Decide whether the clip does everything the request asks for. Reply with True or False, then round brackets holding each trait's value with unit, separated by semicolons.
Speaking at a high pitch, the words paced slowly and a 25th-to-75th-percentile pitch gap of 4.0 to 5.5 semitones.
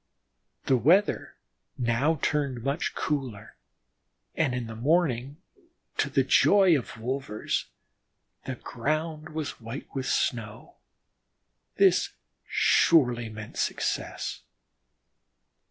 False (130 Hz; 100 wpm; 4.6 semitones)